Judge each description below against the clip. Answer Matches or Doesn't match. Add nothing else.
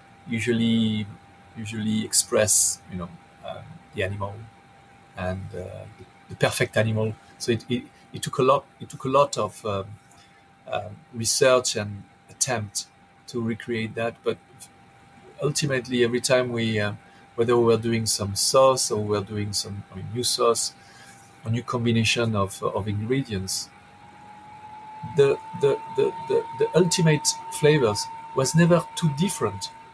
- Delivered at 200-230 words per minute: Doesn't match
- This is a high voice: Doesn't match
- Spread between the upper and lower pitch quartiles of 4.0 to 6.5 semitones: Matches